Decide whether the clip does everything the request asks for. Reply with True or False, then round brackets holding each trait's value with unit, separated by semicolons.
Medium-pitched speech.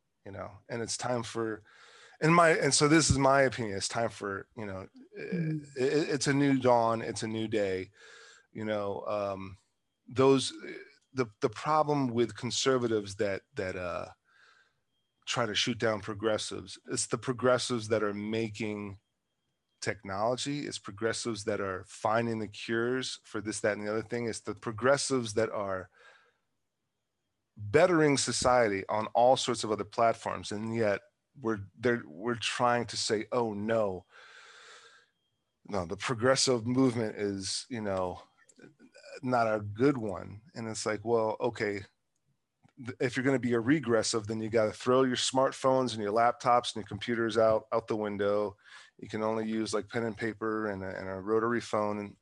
False (115 Hz)